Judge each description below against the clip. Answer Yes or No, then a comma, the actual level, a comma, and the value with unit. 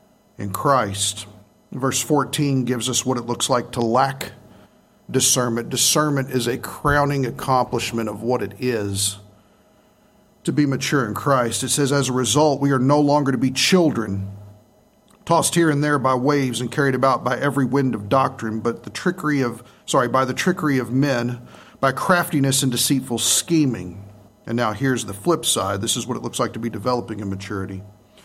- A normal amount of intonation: Yes, average, 3.7 semitones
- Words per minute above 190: No, average, 180 wpm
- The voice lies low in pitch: Yes, low, 130 Hz